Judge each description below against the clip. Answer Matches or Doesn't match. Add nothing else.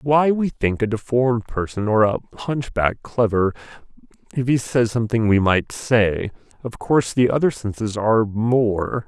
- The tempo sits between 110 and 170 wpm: Matches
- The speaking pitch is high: Doesn't match